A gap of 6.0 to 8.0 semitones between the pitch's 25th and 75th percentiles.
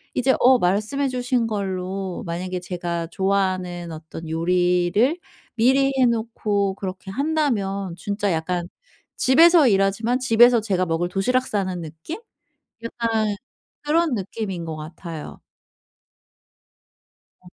No: average, 5.2 semitones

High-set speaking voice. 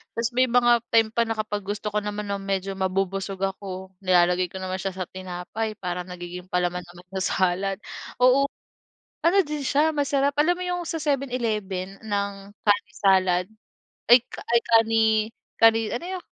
Yes: high, 200 Hz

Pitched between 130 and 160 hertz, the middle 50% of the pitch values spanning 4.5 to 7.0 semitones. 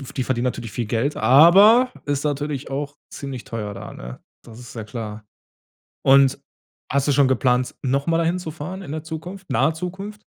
Yes: medium, 140 Hz; average, 4.8 semitones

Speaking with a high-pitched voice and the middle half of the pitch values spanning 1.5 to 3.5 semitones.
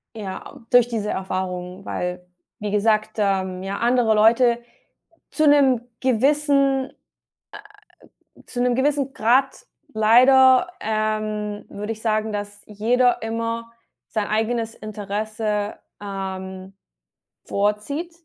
Yes: high, 220 Hz; average, 3.2 semitones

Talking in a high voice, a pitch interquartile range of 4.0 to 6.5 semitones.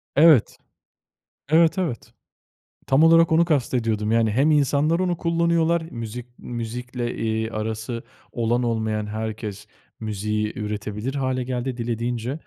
No: low, 120 Hz; average, 5.2 semitones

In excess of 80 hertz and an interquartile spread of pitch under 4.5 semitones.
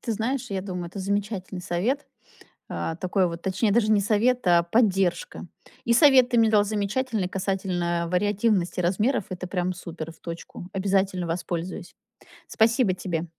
Yes: high, 190 Hz; average, 3.5 semitones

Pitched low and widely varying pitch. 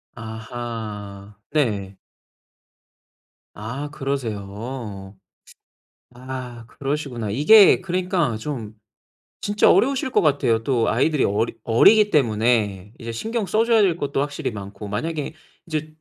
Yes: low, 120 Hz; wide, 6.0 semitones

